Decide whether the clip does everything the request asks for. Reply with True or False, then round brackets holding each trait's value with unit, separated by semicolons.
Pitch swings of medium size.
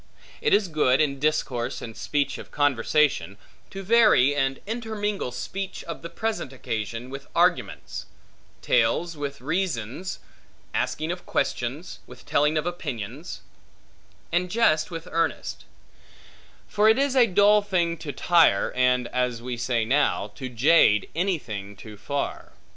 False (6.2 semitones)